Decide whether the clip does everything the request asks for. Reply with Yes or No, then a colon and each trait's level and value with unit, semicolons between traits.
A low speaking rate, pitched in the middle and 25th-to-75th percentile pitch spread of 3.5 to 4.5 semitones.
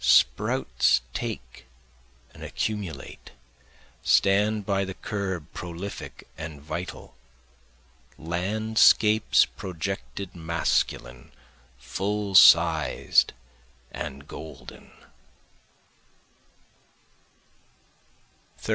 No: slow, 60 wpm; very low, 90 Hz; average, 4.2 semitones